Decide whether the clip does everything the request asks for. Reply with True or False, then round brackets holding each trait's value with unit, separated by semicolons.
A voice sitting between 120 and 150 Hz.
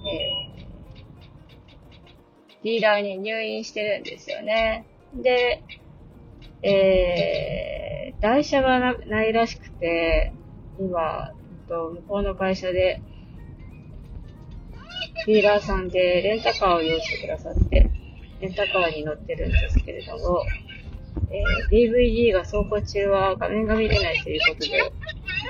False (200 Hz)